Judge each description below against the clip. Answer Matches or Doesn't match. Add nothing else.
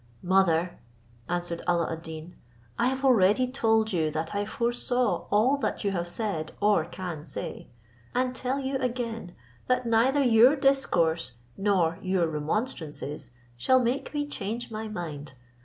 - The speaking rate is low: Doesn't match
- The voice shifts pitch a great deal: Matches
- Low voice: Doesn't match